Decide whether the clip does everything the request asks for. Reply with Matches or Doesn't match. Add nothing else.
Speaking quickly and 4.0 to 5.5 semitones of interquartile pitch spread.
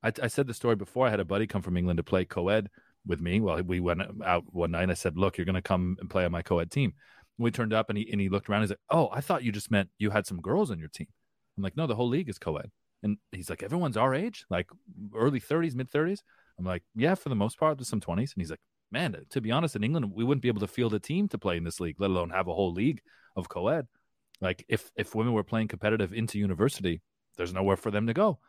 Matches